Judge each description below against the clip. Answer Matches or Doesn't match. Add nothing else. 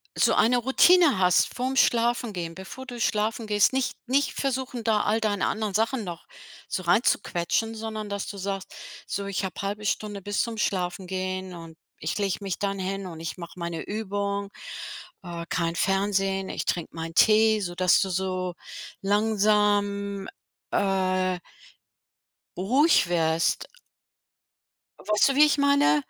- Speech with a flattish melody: Doesn't match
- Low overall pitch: Doesn't match